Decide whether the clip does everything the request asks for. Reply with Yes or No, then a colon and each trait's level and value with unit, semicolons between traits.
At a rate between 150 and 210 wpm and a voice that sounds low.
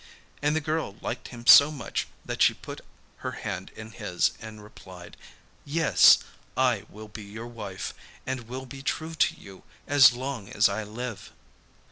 Yes: average, 165 wpm; low, 120 Hz